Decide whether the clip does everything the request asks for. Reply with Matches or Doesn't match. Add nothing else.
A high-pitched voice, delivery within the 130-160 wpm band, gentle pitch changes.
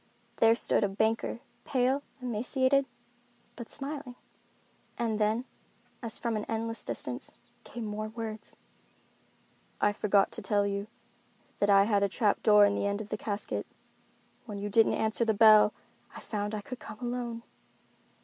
Matches